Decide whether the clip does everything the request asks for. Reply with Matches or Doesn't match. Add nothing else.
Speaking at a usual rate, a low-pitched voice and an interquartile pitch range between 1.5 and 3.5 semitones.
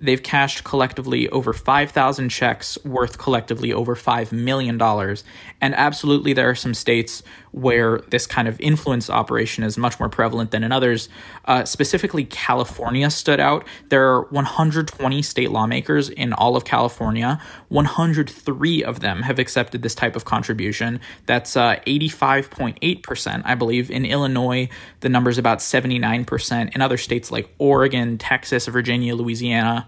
Matches